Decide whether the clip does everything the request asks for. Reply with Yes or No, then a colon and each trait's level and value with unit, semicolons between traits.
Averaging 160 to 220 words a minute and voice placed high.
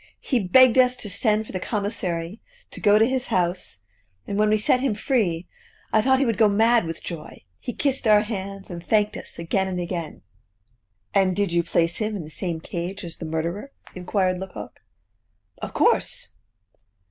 Yes: average, 185 wpm; high, 200 Hz